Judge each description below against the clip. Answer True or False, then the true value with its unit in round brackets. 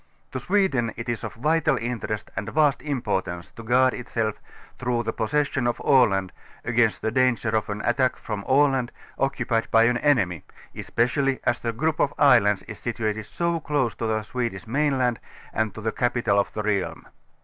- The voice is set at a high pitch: False (120 Hz)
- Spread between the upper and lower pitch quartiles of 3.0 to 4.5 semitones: True (3.4 semitones)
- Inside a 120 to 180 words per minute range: True (175 wpm)